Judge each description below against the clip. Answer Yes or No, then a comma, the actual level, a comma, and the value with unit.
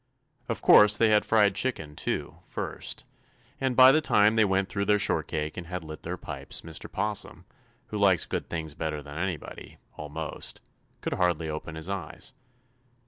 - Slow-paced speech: No, average, 170 wpm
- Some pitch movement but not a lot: Yes, average, 4.8 semitones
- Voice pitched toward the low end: Yes, very low, 90 Hz